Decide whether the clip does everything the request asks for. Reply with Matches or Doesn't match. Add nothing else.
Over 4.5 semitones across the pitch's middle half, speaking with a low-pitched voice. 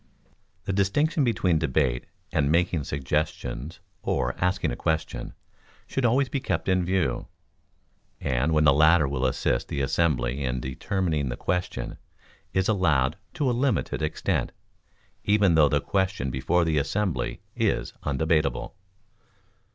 Matches